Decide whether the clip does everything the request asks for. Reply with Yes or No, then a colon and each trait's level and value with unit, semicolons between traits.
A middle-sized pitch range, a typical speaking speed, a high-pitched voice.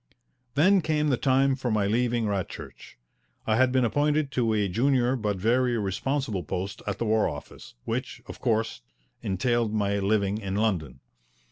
No: average, 4.3 semitones; average, 160 wpm; low, 115 Hz